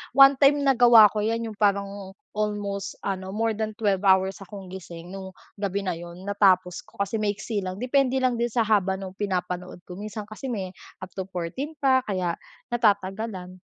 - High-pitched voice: Yes, high, 200 Hz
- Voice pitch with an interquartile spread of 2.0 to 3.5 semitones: Yes, average, 3.0 semitones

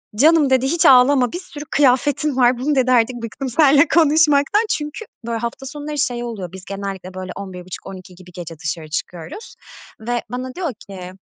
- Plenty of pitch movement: Yes, wide, 7.2 semitones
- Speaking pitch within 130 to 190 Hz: No, very high, 250 Hz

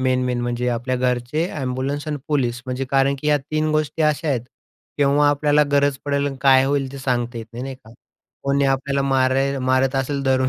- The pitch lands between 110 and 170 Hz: Yes, low, 135 Hz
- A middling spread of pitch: No, narrow, 1.9 semitones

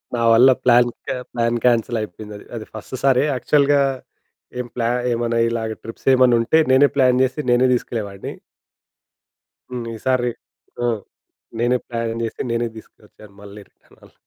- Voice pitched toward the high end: No, low, 120 Hz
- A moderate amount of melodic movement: No, narrow, 1.9 semitones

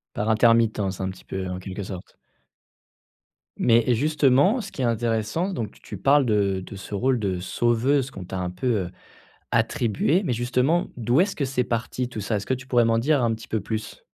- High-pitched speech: No, low, 115 Hz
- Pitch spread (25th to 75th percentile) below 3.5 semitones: No, average, 4.2 semitones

